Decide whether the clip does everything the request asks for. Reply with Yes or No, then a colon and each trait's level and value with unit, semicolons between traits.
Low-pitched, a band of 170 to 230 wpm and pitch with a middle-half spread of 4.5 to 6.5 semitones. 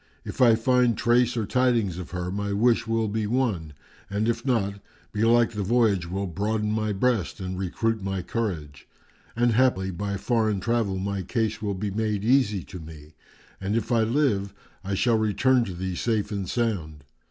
No: low, 105 Hz; average, 180 wpm; average, 3.4 semitones